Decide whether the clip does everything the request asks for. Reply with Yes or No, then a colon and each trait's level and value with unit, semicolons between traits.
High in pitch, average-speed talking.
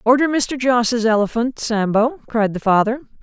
Yes: high, 235 Hz; average, 150 wpm